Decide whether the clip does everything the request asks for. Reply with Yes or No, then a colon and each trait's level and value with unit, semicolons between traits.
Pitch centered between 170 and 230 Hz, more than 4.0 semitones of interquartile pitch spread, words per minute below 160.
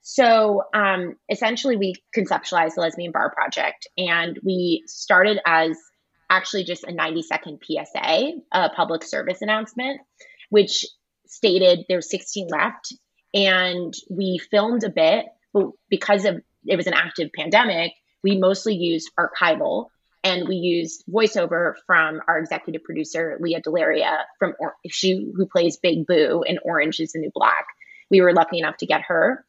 No: medium, 185 Hz; average, 3.7 semitones; average, 150 wpm